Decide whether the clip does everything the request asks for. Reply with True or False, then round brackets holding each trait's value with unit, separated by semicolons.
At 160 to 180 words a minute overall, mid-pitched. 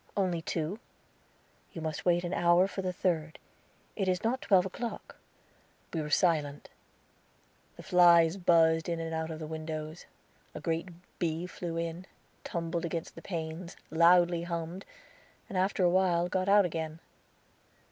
False (150 wpm; 170 Hz)